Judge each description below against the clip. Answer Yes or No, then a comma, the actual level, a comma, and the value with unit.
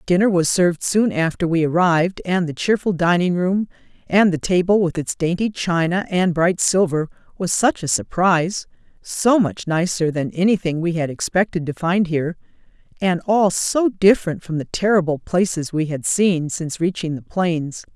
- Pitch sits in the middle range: Yes, medium, 175 Hz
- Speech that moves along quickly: No, average, 170 wpm